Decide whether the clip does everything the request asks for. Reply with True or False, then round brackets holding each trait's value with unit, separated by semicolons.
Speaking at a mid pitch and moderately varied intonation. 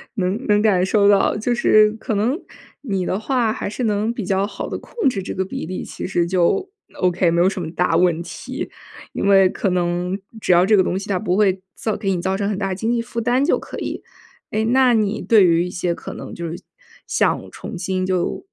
False (195 Hz; 3.3 semitones)